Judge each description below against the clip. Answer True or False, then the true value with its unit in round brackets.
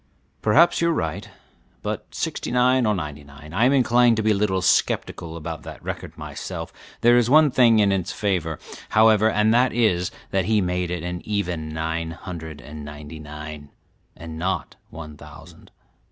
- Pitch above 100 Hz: False (90 Hz)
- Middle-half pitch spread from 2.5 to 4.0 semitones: False (5.6 semitones)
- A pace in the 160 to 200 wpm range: True (180 wpm)